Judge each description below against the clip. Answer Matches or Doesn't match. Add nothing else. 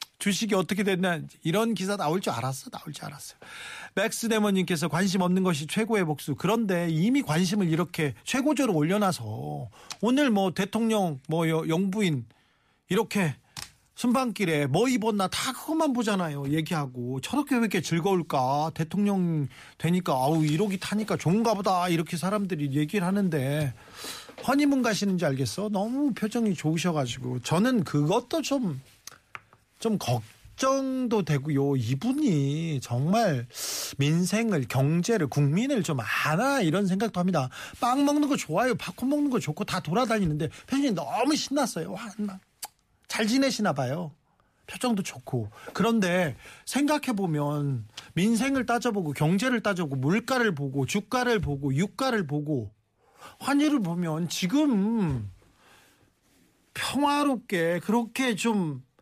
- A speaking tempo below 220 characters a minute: Doesn't match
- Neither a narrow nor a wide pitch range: Doesn't match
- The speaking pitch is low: Doesn't match